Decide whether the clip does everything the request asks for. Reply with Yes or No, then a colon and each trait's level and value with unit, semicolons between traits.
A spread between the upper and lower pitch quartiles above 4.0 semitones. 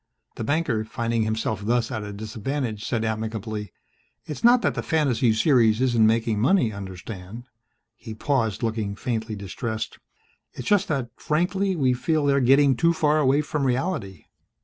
Yes: average, 4.6 semitones